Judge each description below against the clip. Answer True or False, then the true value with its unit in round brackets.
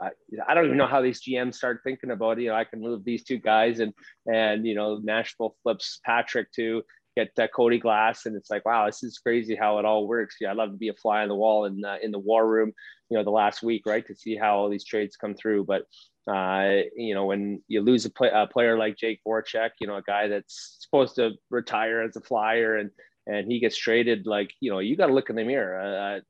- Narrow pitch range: True (1.7 semitones)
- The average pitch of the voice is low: True (110 Hz)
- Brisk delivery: True (260 wpm)